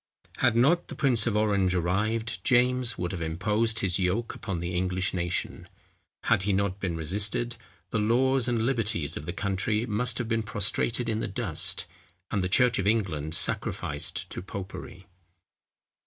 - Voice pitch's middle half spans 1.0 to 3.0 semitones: No, average, 4.0 semitones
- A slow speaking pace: No, average, 165 wpm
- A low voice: Yes, low, 100 Hz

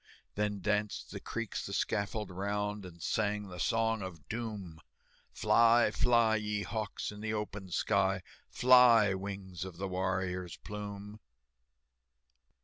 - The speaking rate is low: Yes, slow, 130 wpm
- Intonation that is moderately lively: No, narrow, 2.3 semitones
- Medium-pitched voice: No, low, 105 Hz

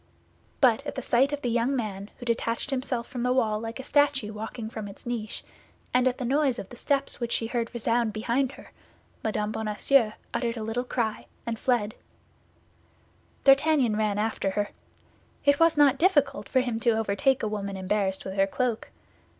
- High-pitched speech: Yes, high, 235 Hz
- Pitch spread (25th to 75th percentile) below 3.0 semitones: No, average, 3.6 semitones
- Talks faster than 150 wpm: Yes, average, 185 wpm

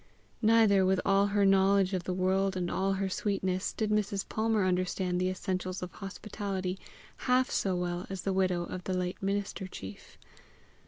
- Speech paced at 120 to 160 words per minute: No, average, 170 wpm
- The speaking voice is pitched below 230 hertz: Yes, high, 190 Hz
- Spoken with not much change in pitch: Yes, narrow, 1.5 semitones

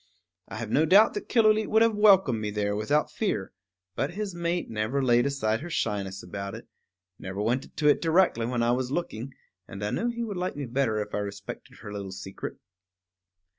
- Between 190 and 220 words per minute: Yes, fast, 205 wpm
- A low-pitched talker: Yes, low, 125 Hz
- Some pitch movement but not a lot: No, wide, 8.9 semitones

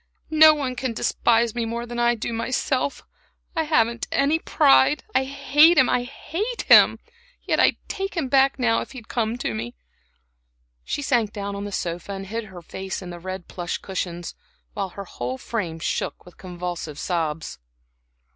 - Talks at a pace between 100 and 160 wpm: No, average, 175 wpm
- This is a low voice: No, high, 225 Hz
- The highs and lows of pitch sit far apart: Yes, wide, 6.7 semitones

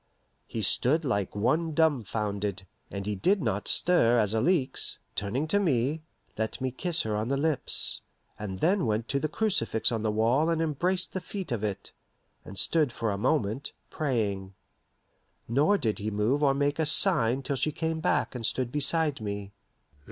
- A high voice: No, low, 130 Hz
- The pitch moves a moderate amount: No, wide, 6.8 semitones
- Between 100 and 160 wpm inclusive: No, average, 175 wpm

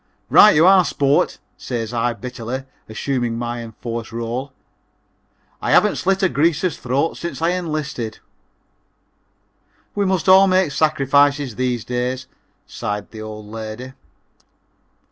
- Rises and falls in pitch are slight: No, wide, 5.4 semitones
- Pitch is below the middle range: Yes, low, 130 Hz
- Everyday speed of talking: No, slow, 125 wpm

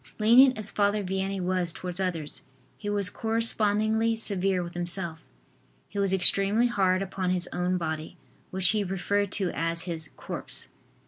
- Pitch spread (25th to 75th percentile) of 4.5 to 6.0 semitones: No, narrow, 2.6 semitones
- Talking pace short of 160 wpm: Yes, average, 150 wpm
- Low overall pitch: No, high, 190 Hz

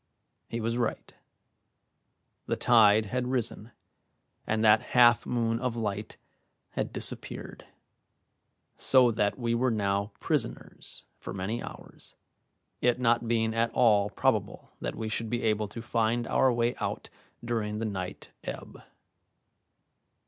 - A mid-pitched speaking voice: No, low, 115 Hz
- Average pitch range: No, narrow, 1.9 semitones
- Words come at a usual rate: No, slow, 130 wpm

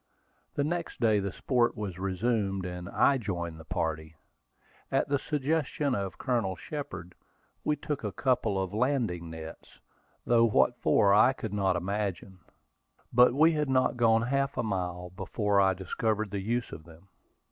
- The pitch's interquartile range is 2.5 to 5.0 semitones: No, wide, 5.5 semitones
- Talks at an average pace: Yes, average, 160 wpm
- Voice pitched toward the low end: Yes, low, 105 Hz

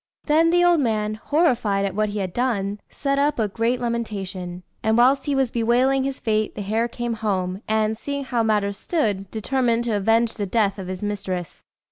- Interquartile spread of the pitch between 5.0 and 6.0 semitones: No, average, 3.8 semitones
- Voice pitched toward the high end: Yes, high, 220 Hz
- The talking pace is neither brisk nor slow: Yes, average, 195 wpm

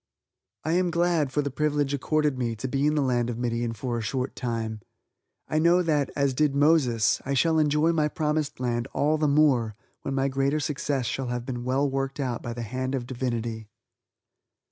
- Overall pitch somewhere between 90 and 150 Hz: Yes, low, 135 Hz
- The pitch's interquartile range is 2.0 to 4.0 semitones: Yes, average, 3.7 semitones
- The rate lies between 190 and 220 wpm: Yes, average, 200 wpm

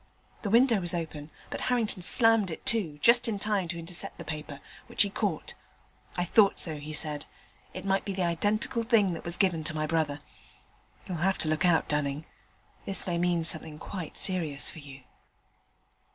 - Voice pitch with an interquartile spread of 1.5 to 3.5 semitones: No, average, 4.3 semitones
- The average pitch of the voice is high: No, medium, 175 Hz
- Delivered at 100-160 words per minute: No, average, 185 wpm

